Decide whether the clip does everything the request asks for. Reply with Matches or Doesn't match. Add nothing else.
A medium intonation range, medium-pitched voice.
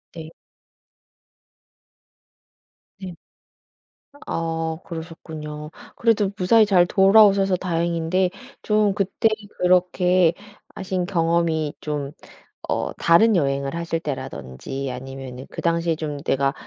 Matches